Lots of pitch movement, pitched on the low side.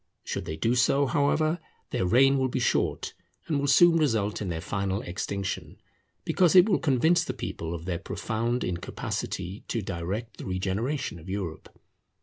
Yes: wide, 6.9 semitones; low, 110 Hz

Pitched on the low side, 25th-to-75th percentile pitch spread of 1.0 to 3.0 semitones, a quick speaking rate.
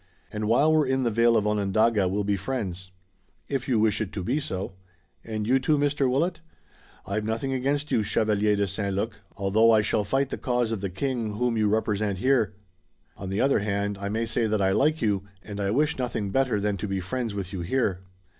No: low, 110 Hz; average, 4.0 semitones; fast, 220 wpm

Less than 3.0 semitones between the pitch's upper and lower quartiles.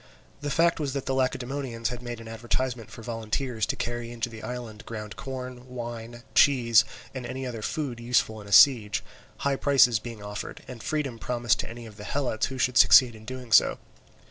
Yes: narrow, 2.4 semitones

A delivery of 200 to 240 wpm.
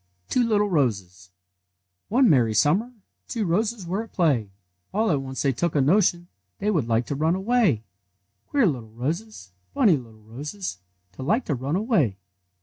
No: average, 170 wpm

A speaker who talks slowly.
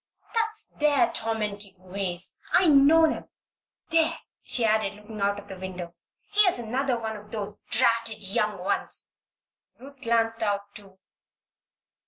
Yes: slow, 130 wpm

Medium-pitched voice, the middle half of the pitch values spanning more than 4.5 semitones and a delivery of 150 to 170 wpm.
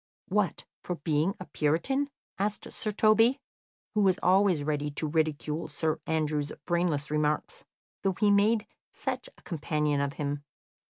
No: medium, 160 Hz; average, 5.2 semitones; average, 140 wpm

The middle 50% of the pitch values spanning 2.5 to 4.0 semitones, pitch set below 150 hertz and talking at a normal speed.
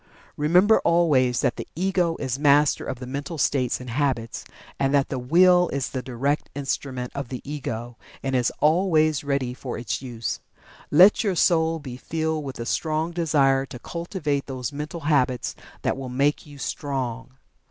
Yes: average, 3.7 semitones; medium, 140 Hz; average, 170 wpm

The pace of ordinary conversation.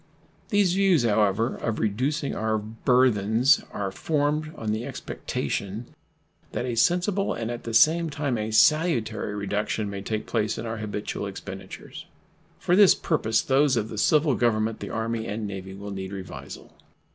Yes: average, 155 wpm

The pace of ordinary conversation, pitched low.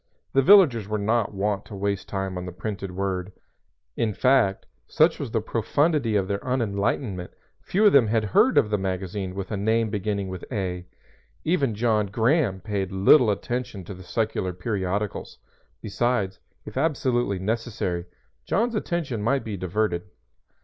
Yes: average, 155 wpm; low, 105 Hz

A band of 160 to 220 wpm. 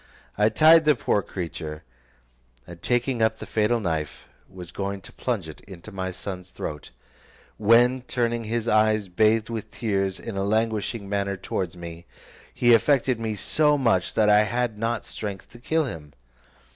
Yes: average, 165 wpm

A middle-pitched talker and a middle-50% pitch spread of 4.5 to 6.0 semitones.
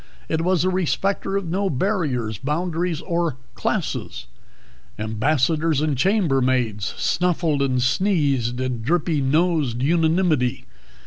Yes: medium, 155 Hz; wide, 5.4 semitones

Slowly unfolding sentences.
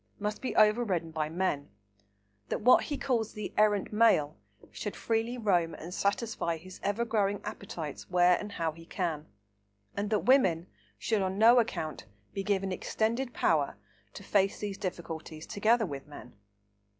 No: average, 155 wpm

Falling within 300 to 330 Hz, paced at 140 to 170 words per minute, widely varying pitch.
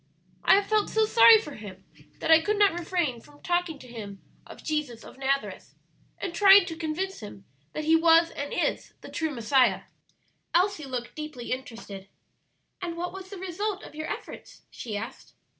No: very high, 320 Hz; average, 180 wpm; wide, 6.6 semitones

